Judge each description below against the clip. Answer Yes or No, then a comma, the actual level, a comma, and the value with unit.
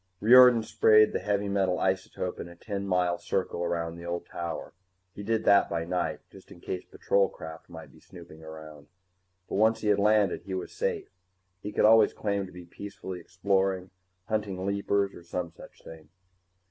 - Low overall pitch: Yes, very low, 95 Hz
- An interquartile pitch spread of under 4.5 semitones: Yes, average, 3.0 semitones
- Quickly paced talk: No, average, 185 wpm